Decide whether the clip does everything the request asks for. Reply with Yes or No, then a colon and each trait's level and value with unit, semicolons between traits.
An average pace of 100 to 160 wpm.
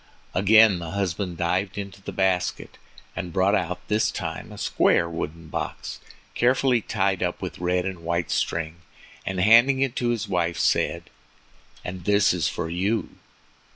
Yes: average, 155 wpm